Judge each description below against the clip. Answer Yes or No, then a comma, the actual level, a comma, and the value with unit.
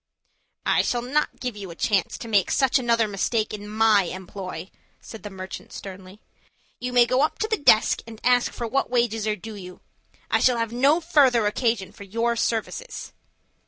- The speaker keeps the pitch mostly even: No, average, 3.4 semitones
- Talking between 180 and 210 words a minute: Yes, average, 190 wpm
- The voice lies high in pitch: Yes, high, 225 Hz